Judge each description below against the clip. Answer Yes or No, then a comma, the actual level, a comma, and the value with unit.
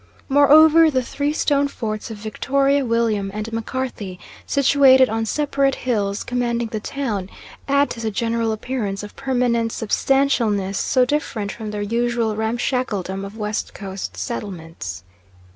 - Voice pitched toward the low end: No, high, 230 Hz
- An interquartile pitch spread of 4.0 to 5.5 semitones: Yes, average, 4.3 semitones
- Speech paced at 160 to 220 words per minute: No, slow, 135 wpm